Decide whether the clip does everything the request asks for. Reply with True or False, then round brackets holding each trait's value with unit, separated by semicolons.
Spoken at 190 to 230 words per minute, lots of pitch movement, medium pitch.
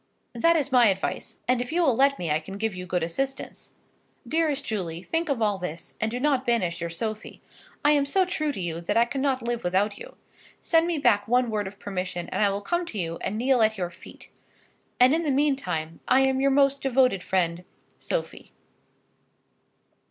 False (205 wpm; 6.6 semitones; 235 Hz)